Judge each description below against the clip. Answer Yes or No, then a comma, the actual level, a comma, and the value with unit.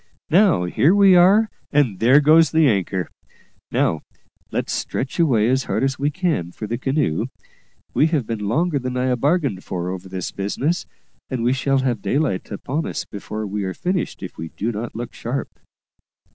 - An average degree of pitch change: No, wide, 6.7 semitones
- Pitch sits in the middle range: No, low, 130 Hz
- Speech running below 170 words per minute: No, average, 180 wpm